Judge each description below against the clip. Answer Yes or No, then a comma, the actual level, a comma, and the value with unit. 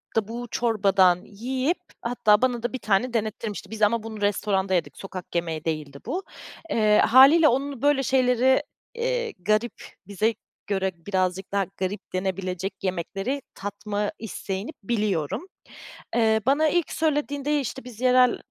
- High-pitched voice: Yes, high, 220 Hz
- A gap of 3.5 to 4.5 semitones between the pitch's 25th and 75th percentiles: No, average, 4.9 semitones